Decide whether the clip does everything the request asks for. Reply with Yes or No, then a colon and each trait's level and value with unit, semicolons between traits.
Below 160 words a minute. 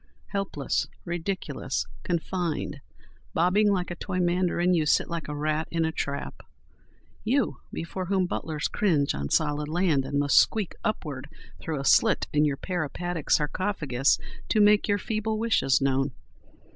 Yes: average, 140 wpm